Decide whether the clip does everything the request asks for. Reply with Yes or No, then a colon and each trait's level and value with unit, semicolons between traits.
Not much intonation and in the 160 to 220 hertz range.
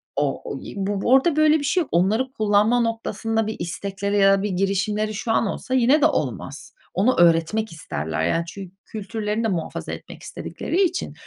No: average, 4.0 semitones; high, 210 Hz